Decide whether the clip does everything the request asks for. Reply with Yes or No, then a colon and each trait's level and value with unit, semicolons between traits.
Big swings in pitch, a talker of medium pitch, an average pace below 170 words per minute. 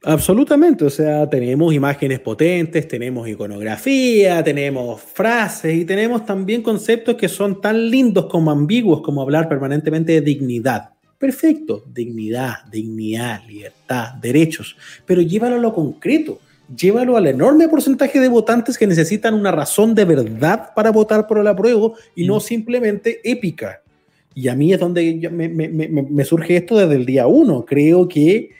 Yes: wide, 7.9 semitones; medium, 170 Hz; average, 155 wpm